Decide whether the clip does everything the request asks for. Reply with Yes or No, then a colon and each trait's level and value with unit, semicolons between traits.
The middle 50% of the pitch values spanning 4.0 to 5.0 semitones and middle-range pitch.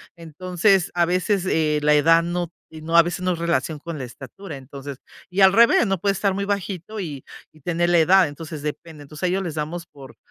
No: average, 3.3 semitones; medium, 170 Hz